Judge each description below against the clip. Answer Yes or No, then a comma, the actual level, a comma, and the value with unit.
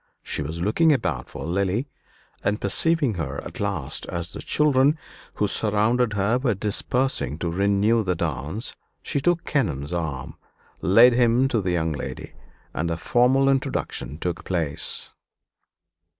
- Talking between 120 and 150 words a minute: Yes, average, 145 wpm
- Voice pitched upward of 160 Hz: No, low, 100 Hz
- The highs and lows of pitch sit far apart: Yes, wide, 6.9 semitones